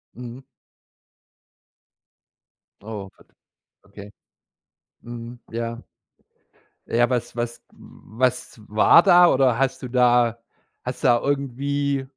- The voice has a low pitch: Yes, low, 120 Hz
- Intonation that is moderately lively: No, narrow, 2.3 semitones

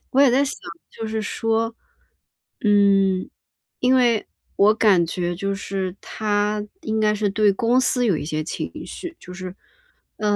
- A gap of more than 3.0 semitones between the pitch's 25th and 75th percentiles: No, narrow, 2.6 semitones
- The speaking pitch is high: Yes, high, 210 Hz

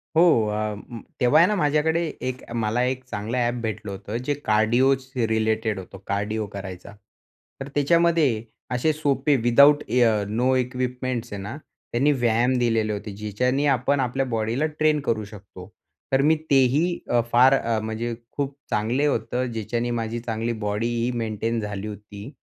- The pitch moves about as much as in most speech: Yes, average, 3.6 semitones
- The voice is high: No, low, 120 Hz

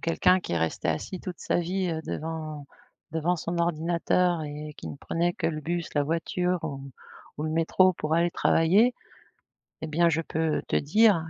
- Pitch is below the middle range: No, medium, 165 Hz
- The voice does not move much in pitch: Yes, narrow, 2.2 semitones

